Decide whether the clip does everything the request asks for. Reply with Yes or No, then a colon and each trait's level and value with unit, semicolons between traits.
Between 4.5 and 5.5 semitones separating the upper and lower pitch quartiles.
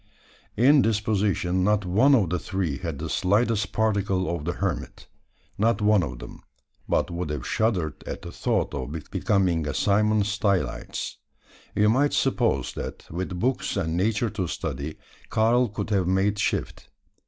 No: average, 4.0 semitones